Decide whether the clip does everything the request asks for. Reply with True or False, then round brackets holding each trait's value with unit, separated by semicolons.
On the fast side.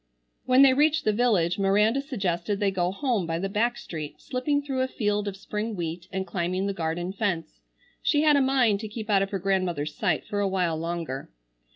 True (210 wpm)